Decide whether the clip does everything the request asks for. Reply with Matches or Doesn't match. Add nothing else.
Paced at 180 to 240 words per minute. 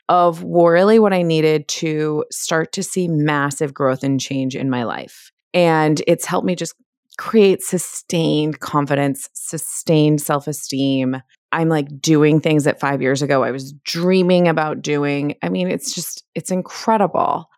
Doesn't match